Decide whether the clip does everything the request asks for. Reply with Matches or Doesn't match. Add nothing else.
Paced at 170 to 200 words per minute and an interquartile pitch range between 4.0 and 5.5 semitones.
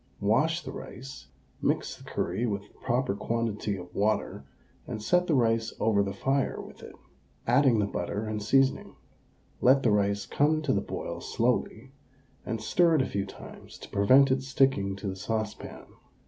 Matches